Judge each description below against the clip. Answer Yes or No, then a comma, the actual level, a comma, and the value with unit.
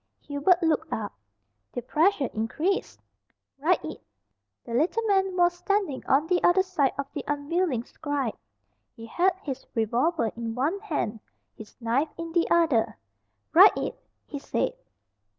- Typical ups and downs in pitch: No, wide, 6.3 semitones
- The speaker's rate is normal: Yes, average, 145 wpm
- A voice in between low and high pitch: No, very high, 305 Hz